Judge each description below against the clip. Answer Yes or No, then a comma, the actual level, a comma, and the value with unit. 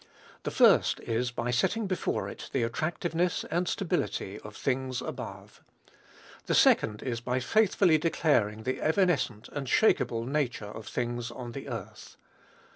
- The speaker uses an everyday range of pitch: No, wide, 5.9 semitones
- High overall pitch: No, low, 130 Hz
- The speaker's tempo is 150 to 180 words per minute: No, average, 140 wpm